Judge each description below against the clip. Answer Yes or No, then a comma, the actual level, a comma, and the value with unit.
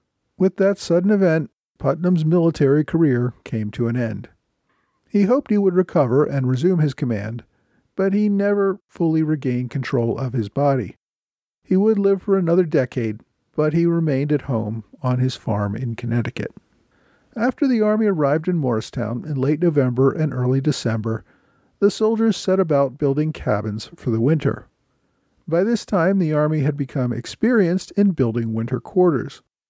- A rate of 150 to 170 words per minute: Yes, average, 160 wpm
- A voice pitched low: No, medium, 145 Hz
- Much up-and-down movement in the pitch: Yes, wide, 7.1 semitones